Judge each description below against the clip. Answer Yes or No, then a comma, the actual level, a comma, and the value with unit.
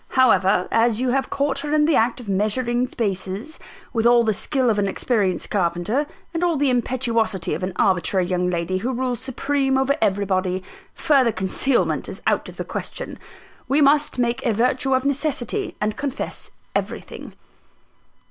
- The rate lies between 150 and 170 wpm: Yes, average, 165 wpm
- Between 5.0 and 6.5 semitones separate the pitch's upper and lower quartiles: Yes, wide, 5.4 semitones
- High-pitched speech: Yes, high, 240 Hz